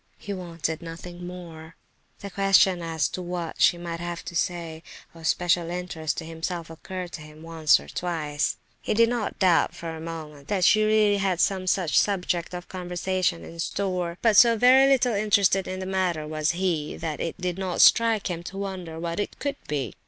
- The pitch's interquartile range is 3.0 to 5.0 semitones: No, narrow, 2.6 semitones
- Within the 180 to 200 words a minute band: Yes, average, 195 wpm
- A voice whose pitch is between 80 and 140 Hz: No, medium, 175 Hz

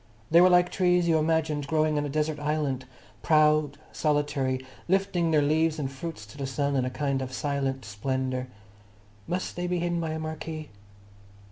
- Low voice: No, medium, 150 Hz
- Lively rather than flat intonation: No, average, 2.9 semitones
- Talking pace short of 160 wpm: No, average, 175 wpm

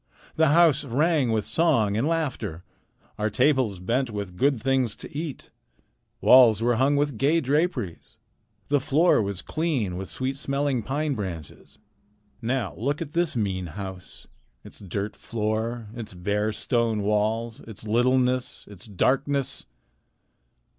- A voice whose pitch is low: Yes, low, 120 Hz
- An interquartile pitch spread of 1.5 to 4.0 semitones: No, average, 5.1 semitones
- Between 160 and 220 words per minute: No, slow, 135 wpm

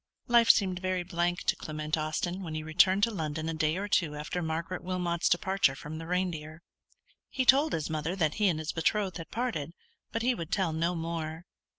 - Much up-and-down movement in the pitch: No, average, 3.0 semitones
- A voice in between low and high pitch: Yes, medium, 170 Hz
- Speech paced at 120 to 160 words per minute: No, fast, 205 wpm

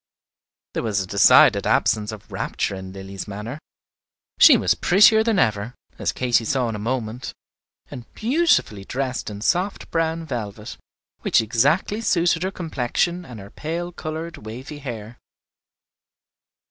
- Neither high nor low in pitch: No, low, 125 Hz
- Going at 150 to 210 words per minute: No, average, 140 wpm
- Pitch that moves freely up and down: Yes, wide, 7.9 semitones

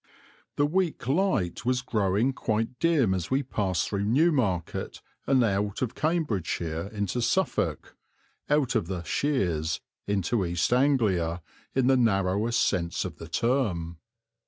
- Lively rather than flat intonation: Yes, wide, 6.4 semitones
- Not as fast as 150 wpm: Yes, slow, 135 wpm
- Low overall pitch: Yes, low, 110 Hz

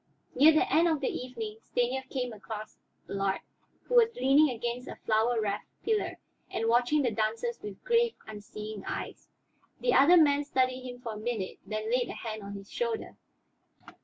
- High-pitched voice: Yes, high, 245 Hz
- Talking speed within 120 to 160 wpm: No, average, 175 wpm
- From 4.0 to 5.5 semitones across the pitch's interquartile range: Yes, average, 4.8 semitones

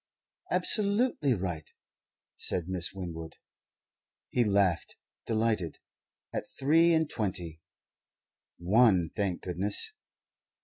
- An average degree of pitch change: No, wide, 6.1 semitones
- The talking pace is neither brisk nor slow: No, slow, 85 wpm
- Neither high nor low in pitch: No, low, 100 Hz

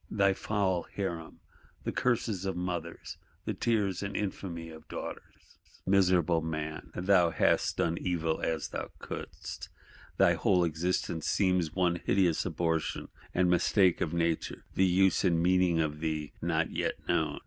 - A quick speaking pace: No, average, 145 wpm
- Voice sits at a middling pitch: No, very low, 90 Hz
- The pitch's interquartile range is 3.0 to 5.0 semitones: No, narrow, 2.5 semitones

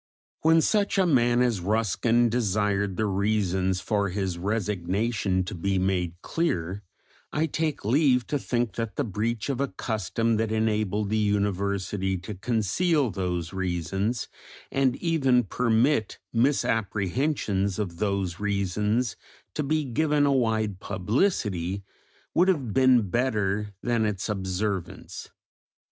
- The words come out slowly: Yes, slow, 125 wpm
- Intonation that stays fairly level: No, average, 4.2 semitones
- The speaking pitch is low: Yes, low, 105 Hz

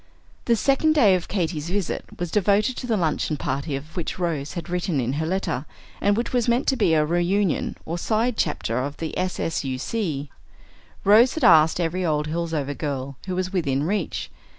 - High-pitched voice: No, medium, 175 Hz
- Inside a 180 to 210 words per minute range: Yes, average, 185 wpm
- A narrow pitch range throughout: No, average, 5.2 semitones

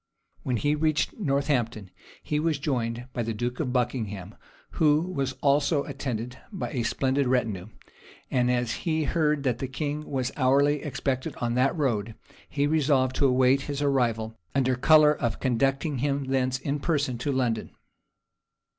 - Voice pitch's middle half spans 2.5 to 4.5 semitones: Yes, average, 3.0 semitones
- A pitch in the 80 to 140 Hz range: Yes, low, 135 Hz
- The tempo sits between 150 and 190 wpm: Yes, average, 155 wpm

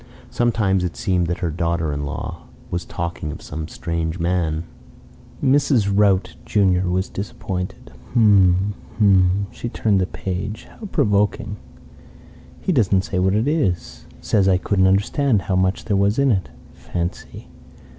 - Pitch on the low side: Yes, very low, 95 Hz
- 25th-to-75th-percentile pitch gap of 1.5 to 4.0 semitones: Yes, average, 2.7 semitones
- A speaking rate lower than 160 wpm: Yes, average, 145 wpm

